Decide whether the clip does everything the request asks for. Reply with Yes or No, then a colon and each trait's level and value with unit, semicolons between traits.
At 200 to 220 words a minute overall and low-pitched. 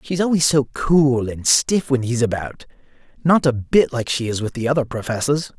Yes: fast, 205 wpm; low, 130 Hz